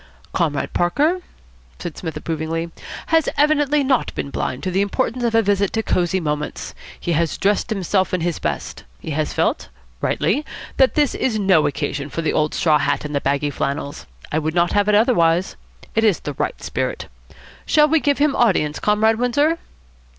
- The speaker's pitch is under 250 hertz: Yes, medium, 185 Hz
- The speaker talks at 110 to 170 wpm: No, average, 185 wpm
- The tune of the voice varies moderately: No, wide, 7.4 semitones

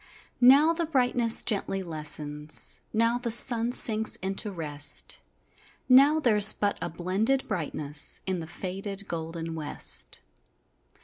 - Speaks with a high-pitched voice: Yes, high, 195 Hz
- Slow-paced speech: Yes, slow, 120 wpm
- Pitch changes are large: Yes, wide, 6.5 semitones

